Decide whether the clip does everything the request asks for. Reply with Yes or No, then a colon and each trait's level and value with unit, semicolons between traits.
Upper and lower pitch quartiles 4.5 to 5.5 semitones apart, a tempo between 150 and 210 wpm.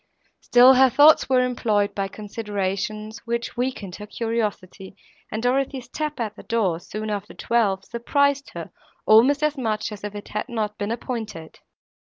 No: average, 3.4 semitones; average, 160 wpm